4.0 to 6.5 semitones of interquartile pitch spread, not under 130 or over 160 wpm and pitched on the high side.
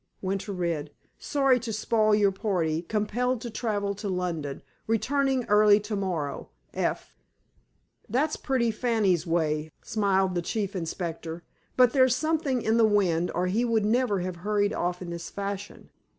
Yes: average, 4.5 semitones; average, 150 wpm; high, 205 Hz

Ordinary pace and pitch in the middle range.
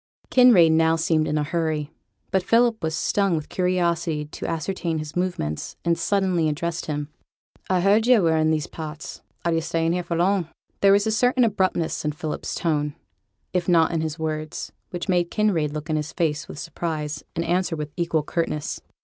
Yes: average, 190 wpm; medium, 165 Hz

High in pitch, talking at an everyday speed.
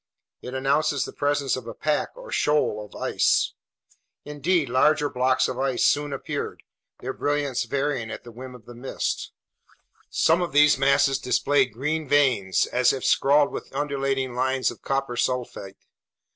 No: low, 135 Hz; average, 160 wpm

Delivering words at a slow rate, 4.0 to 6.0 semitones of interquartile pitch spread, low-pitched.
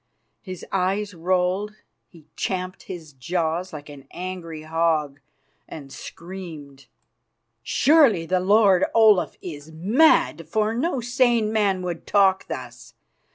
No: slow, 115 wpm; average, 4.5 semitones; medium, 180 Hz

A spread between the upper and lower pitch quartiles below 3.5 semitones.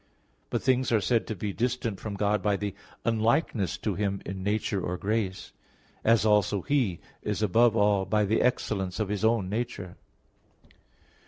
Yes: narrow, 2.6 semitones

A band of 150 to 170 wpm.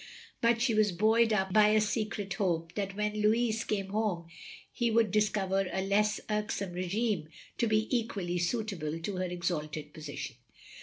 Yes: average, 160 wpm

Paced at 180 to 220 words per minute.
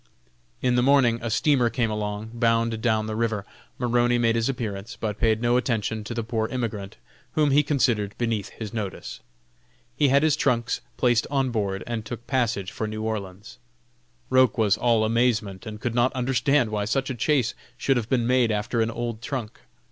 Yes: average, 185 wpm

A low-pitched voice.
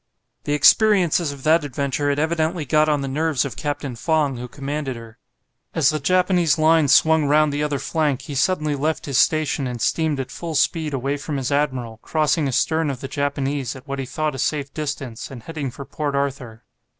No: medium, 145 Hz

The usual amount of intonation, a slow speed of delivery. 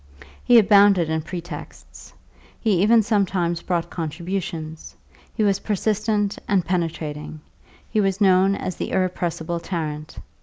Yes: average, 3.5 semitones; slow, 120 wpm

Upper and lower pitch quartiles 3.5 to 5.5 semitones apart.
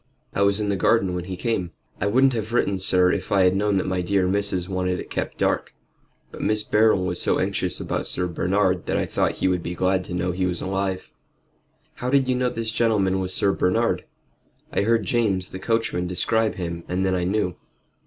No: average, 2.7 semitones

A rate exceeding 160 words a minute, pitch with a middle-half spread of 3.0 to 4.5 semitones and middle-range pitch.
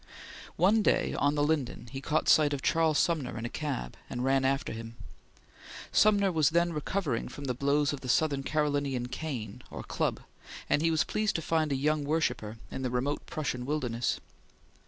Yes: average, 185 wpm; average, 3.6 semitones; medium, 145 Hz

